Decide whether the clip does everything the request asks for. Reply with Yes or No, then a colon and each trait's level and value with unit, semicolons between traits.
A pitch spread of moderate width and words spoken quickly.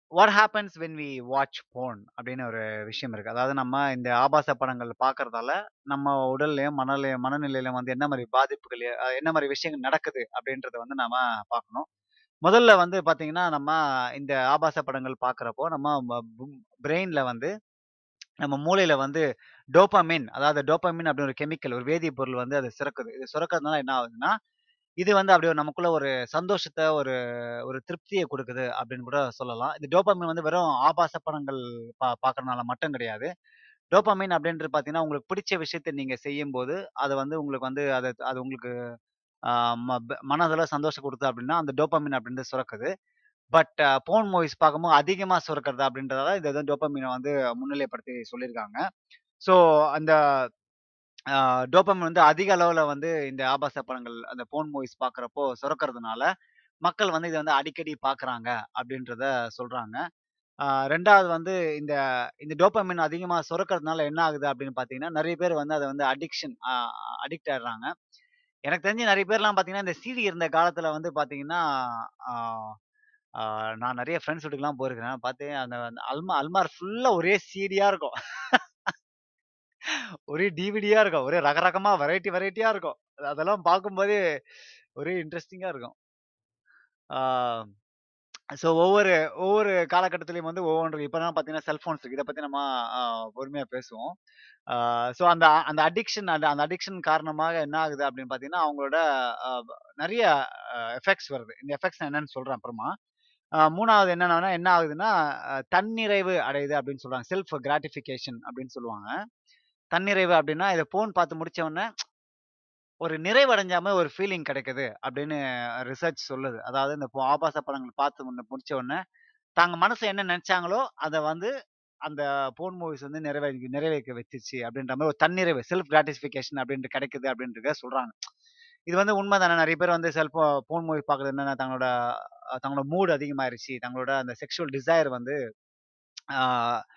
Yes: average, 5.0 semitones; fast, 135 wpm